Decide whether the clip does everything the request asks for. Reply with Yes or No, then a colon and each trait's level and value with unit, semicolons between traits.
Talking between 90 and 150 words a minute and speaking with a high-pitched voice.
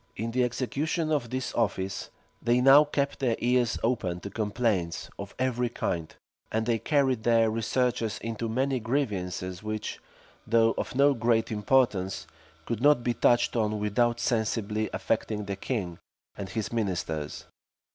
No: average, 145 wpm; low, 115 Hz